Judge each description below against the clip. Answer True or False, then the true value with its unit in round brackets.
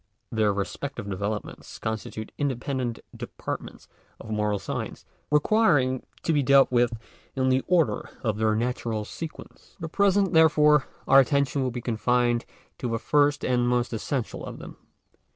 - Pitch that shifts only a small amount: False (4.5 semitones)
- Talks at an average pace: True (150 wpm)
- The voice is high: False (125 Hz)